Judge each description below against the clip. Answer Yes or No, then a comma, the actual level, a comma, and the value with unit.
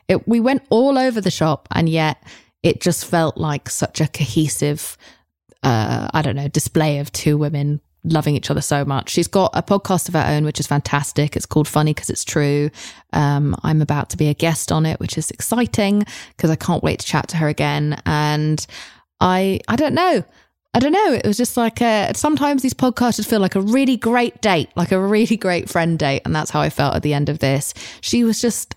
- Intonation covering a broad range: Yes, wide, 6.5 semitones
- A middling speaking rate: No, fast, 220 wpm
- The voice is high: No, medium, 155 Hz